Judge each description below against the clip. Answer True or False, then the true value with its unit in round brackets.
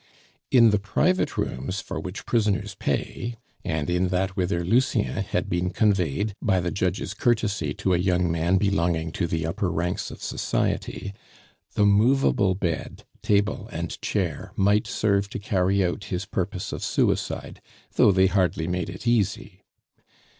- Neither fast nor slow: True (155 wpm)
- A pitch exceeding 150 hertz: False (95 Hz)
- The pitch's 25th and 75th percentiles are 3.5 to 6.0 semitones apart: False (2.6 semitones)